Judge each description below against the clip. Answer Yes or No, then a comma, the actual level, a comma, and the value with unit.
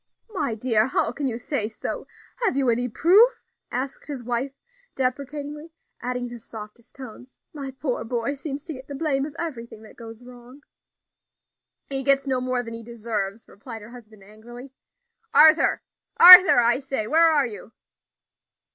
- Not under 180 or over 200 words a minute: No, average, 165 wpm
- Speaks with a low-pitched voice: No, very high, 250 Hz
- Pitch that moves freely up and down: No, average, 3.4 semitones